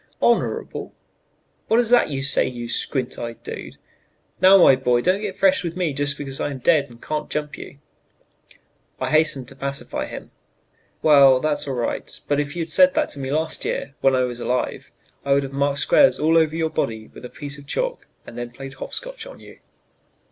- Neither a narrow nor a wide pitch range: Yes, average, 3.7 semitones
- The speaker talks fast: Yes, fast, 210 wpm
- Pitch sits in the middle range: Yes, medium, 145 Hz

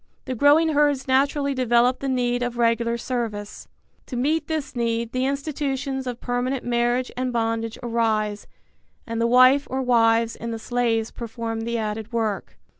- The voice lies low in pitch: No, high, 245 Hz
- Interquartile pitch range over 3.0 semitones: No, narrow, 2.4 semitones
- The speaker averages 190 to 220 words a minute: No, average, 160 wpm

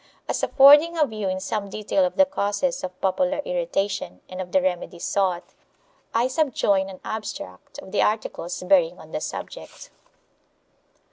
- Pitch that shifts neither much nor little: No, wide, 6.0 semitones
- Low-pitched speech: No, high, 200 Hz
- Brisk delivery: No, average, 160 wpm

